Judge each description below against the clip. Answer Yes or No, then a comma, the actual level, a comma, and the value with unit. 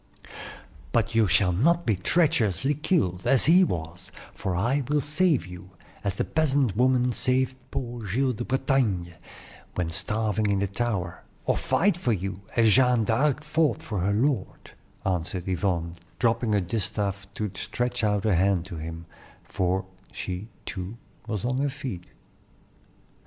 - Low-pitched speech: Yes, low, 110 Hz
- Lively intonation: Yes, wide, 5.8 semitones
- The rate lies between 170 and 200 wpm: No, average, 150 wpm